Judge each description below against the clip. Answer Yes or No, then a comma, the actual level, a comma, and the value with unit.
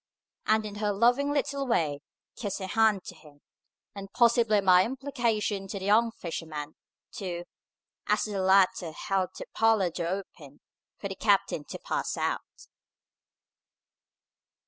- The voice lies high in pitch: Yes, high, 200 Hz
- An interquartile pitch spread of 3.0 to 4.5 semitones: Yes, average, 3.6 semitones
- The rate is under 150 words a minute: Yes, average, 140 wpm